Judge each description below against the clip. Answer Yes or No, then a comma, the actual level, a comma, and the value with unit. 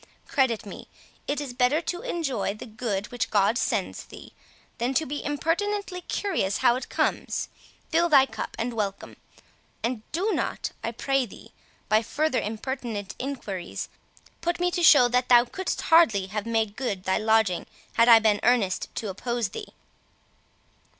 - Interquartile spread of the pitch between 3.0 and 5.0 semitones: No, wide, 5.4 semitones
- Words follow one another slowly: No, average, 160 wpm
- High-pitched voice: Yes, high, 245 Hz